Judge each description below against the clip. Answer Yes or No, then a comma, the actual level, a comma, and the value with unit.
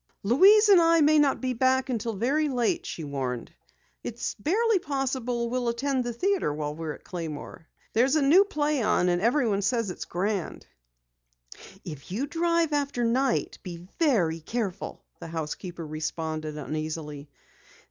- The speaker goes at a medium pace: Yes, average, 150 wpm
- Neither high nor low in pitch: No, high, 235 Hz